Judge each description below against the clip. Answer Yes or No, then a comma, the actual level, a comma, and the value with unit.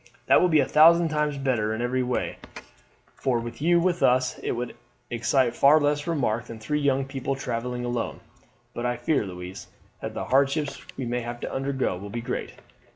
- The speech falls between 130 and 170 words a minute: No, average, 195 wpm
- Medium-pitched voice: No, low, 130 Hz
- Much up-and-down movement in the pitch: No, average, 3.5 semitones